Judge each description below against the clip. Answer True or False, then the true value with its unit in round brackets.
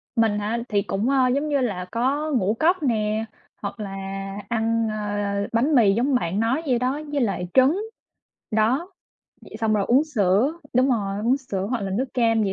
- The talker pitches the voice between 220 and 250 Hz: True (230 Hz)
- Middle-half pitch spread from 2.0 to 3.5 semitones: False (4.2 semitones)